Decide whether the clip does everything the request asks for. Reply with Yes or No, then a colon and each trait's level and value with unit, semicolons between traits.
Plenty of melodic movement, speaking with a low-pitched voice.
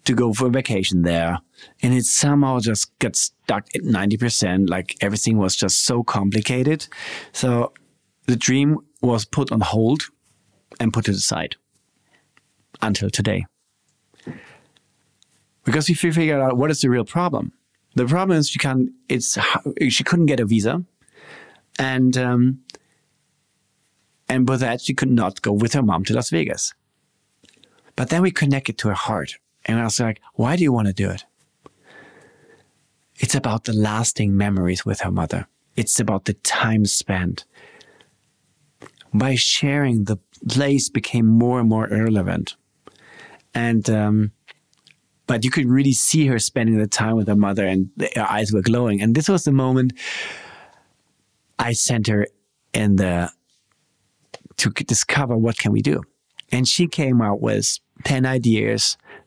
No: average, 3.9 semitones; low, 120 Hz